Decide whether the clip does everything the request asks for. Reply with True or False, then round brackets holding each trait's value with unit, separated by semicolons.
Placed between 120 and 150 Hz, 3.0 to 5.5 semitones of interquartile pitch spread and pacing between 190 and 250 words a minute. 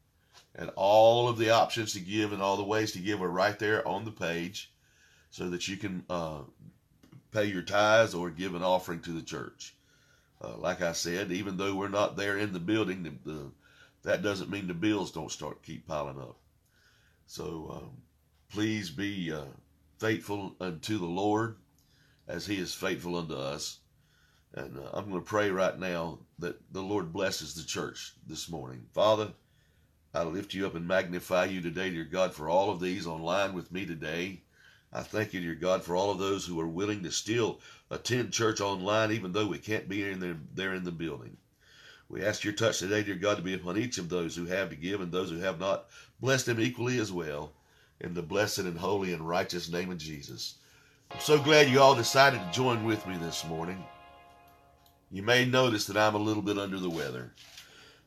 False (95 Hz; 3.6 semitones; 205 wpm)